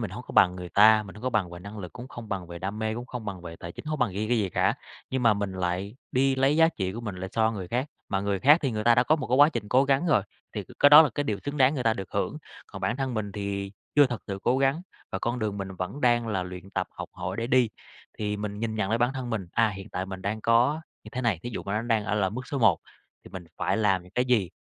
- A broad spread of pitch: No, average, 4.4 semitones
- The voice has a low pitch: Yes, low, 110 Hz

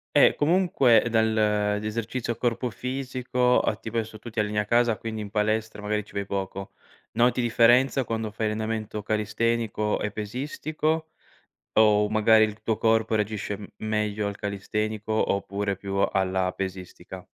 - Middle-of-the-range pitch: No, low, 110 Hz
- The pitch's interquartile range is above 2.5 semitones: No, narrow, 2.0 semitones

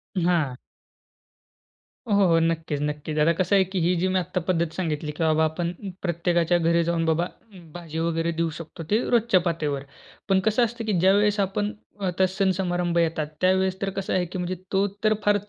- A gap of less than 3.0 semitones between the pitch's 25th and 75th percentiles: Yes, narrow, 2.6 semitones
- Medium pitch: Yes, medium, 175 Hz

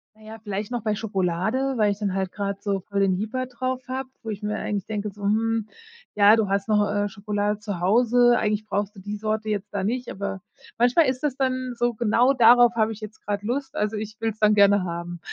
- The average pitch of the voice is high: Yes, high, 215 Hz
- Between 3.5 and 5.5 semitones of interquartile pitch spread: No, average, 2.9 semitones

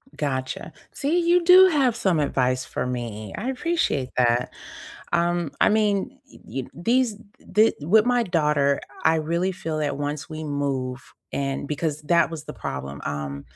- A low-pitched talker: No, medium, 155 Hz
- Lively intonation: Yes, wide, 7.9 semitones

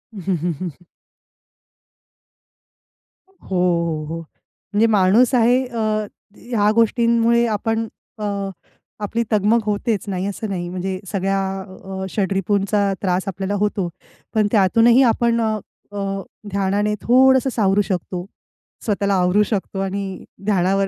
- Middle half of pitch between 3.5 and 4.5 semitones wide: No, average, 2.9 semitones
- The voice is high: Yes, high, 205 Hz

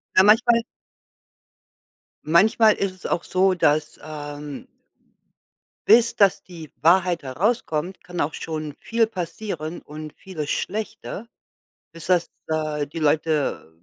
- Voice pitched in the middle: Yes, medium, 165 Hz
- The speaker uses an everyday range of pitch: Yes, average, 4.2 semitones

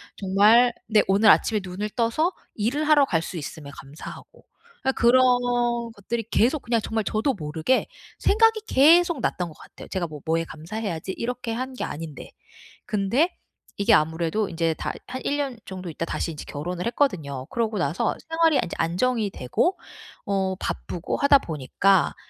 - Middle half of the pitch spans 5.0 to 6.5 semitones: No, wide, 7.2 semitones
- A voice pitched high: Yes, high, 205 Hz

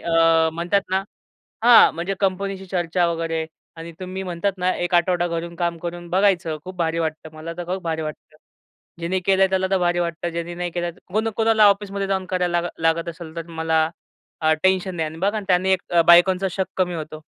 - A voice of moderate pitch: Yes, medium, 175 Hz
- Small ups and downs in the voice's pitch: Yes, narrow, 2.3 semitones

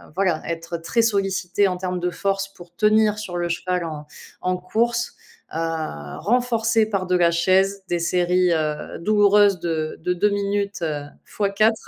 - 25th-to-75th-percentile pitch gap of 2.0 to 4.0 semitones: Yes, average, 3.1 semitones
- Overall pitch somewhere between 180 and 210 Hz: Yes, medium, 185 Hz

